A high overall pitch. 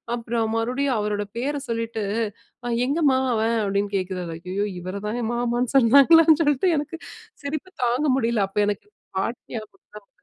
Yes: high, 230 Hz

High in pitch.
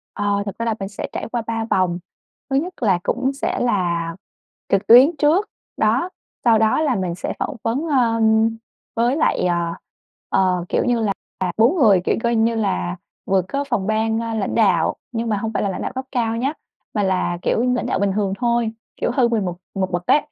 Yes: high, 225 Hz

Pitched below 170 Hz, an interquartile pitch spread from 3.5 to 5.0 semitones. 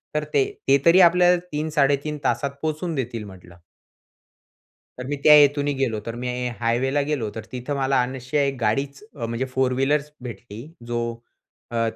Yes: low, 135 Hz; average, 3.8 semitones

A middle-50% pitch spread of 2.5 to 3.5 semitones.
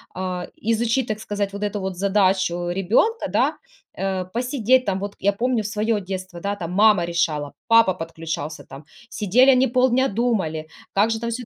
No: average, 3.9 semitones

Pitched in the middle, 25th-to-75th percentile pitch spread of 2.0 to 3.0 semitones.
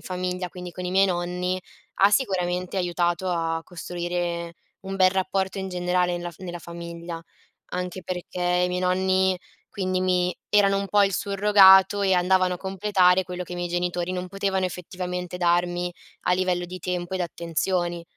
No: medium, 180 Hz; narrow, 1.2 semitones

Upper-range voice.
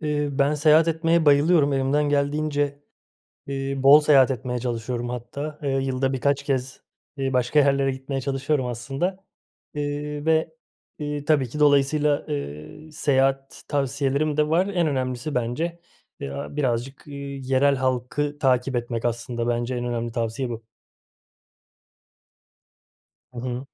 No: low, 135 Hz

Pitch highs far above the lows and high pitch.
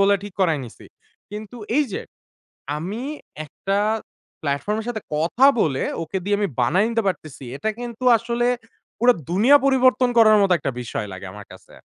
Yes: wide, 7.0 semitones; high, 205 Hz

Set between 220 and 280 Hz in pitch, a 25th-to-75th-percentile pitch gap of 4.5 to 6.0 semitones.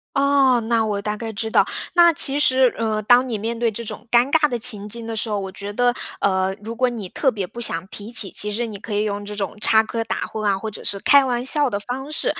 No: high, 225 Hz; average, 3.2 semitones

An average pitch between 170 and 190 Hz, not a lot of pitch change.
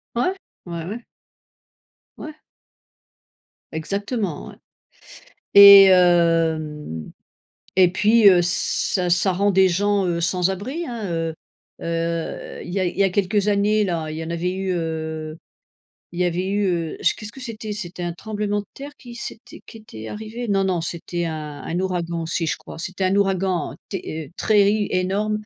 No: medium, 185 Hz; average, 3.6 semitones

